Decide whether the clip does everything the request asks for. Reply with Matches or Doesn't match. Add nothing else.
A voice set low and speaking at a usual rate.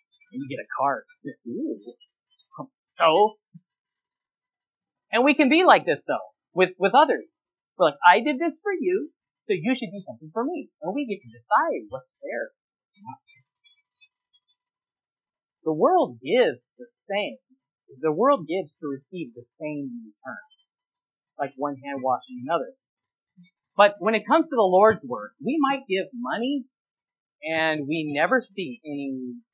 Doesn't match